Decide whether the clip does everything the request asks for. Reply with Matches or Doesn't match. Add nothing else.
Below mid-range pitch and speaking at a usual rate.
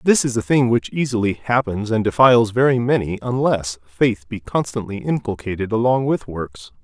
Matches